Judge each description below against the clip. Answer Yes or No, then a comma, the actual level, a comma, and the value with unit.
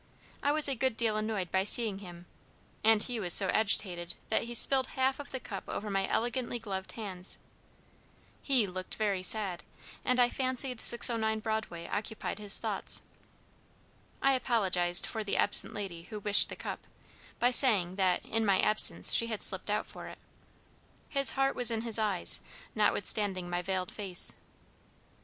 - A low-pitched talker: No, high, 215 Hz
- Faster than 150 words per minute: Yes, average, 165 wpm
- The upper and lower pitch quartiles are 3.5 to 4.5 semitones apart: Yes, average, 3.8 semitones